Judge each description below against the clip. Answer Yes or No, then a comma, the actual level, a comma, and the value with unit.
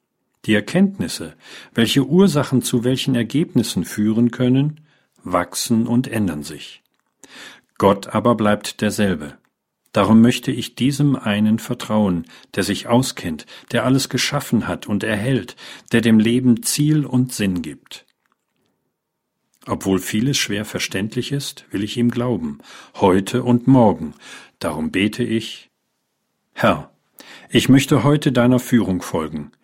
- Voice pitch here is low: Yes, low, 120 Hz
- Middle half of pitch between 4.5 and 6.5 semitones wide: No, average, 3.8 semitones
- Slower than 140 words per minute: Yes, slow, 125 wpm